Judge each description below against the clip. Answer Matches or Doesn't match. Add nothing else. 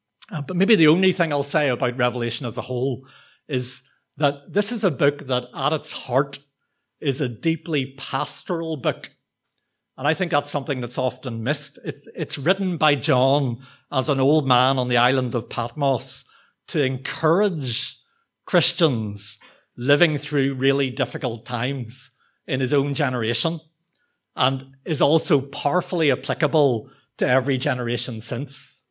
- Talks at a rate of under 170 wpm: Matches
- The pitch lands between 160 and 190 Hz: Doesn't match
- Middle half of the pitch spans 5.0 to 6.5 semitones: Doesn't match